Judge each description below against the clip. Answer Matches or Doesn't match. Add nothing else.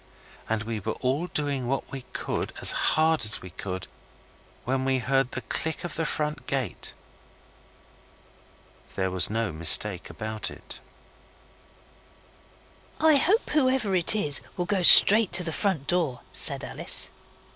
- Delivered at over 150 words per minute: Doesn't match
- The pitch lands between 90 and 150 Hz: Matches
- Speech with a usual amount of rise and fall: Doesn't match